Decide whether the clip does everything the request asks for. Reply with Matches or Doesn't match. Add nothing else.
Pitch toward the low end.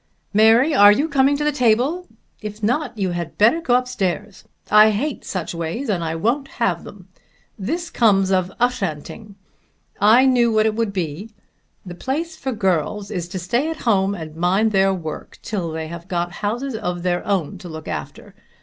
Doesn't match